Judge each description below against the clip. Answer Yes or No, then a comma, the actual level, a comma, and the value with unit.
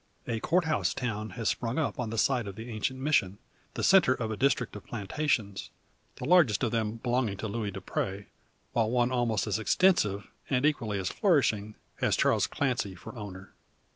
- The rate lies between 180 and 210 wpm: Yes, average, 185 wpm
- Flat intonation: No, average, 4.1 semitones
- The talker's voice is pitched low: Yes, low, 115 Hz